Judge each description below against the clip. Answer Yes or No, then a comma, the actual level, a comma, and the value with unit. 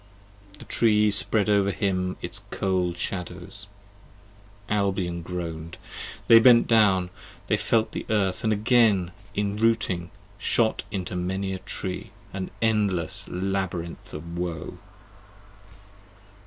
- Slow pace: Yes, slow, 110 wpm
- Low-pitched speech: Yes, very low, 95 Hz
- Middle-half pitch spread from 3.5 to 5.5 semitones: No, average, 2.9 semitones